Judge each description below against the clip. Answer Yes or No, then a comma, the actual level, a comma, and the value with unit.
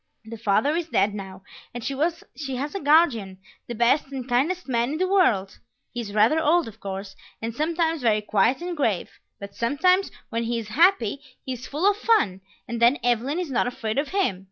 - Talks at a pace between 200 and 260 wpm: Yes, fast, 205 wpm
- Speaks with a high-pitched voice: Yes, very high, 250 Hz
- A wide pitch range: Yes, wide, 6.6 semitones